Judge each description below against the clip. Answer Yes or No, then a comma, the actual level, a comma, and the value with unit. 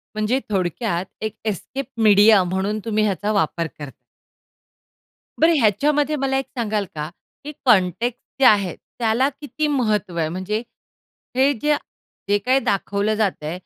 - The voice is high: Yes, high, 215 Hz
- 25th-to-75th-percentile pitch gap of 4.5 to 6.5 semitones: Yes, average, 5.3 semitones